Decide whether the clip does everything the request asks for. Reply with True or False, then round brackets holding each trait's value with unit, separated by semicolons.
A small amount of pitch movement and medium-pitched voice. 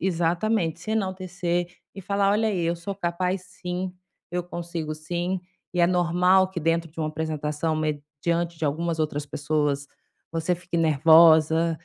True (2.3 semitones; 170 Hz)